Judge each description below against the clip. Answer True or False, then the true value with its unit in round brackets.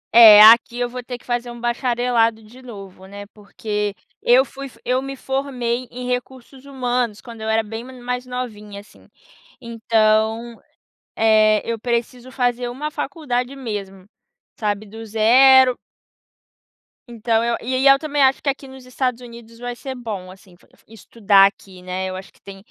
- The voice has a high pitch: True (235 Hz)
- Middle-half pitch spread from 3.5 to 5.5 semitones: False (2.8 semitones)